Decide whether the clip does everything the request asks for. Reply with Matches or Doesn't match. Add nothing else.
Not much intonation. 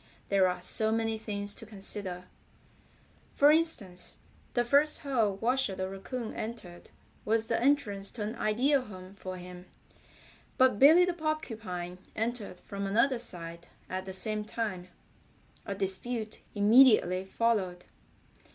Doesn't match